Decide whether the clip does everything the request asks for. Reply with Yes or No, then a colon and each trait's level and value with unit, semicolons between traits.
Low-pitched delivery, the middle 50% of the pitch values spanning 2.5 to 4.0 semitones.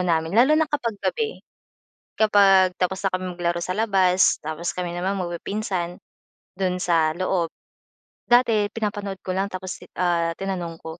No: medium, 185 Hz; average, 2.8 semitones